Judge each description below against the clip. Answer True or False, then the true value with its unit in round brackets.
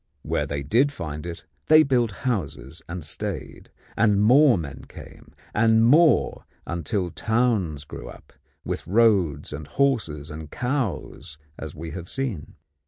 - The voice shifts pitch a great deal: True (7.9 semitones)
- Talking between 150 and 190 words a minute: False (140 wpm)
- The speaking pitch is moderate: False (95 Hz)